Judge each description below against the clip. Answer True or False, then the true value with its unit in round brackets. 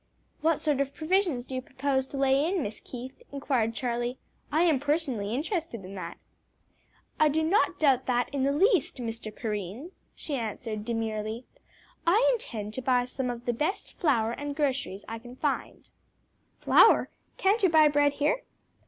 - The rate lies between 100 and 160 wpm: False (170 wpm)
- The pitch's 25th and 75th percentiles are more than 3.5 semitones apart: True (4.6 semitones)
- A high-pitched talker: True (265 Hz)